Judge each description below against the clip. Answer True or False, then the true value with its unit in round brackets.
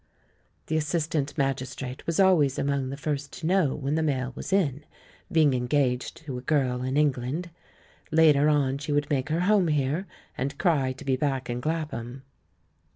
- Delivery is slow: False (170 wpm)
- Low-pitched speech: False (145 Hz)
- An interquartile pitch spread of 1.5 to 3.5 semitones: True (3.1 semitones)